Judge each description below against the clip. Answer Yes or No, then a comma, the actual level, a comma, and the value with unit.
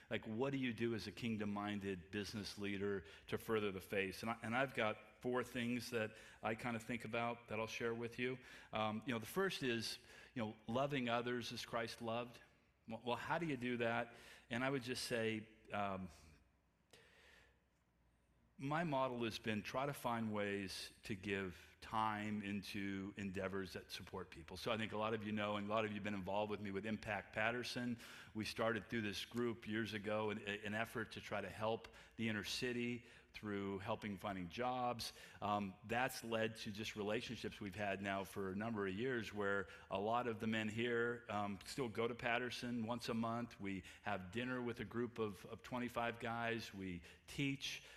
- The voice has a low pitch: Yes, low, 110 Hz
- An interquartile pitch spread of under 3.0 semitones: Yes, narrow, 2.6 semitones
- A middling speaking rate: Yes, average, 195 wpm